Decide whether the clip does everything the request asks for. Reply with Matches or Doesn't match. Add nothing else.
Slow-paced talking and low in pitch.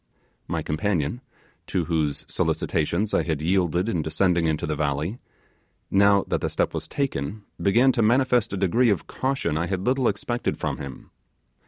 Doesn't match